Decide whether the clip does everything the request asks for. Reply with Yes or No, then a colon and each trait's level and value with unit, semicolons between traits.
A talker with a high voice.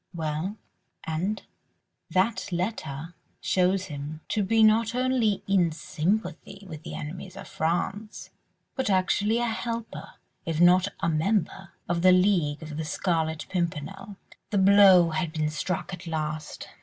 No: medium, 180 Hz